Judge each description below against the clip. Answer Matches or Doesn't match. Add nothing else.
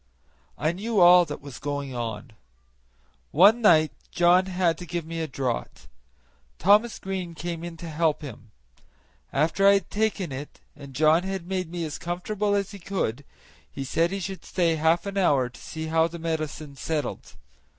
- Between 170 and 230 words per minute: Matches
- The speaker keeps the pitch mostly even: Doesn't match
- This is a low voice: Doesn't match